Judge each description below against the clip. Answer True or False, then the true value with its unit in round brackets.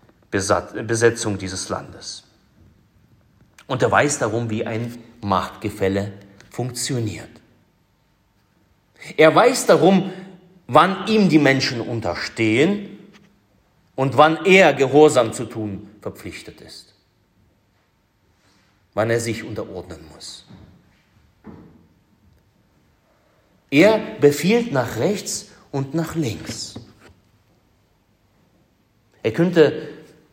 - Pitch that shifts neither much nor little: False (6.3 semitones)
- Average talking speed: False (80 wpm)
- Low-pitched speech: True (115 Hz)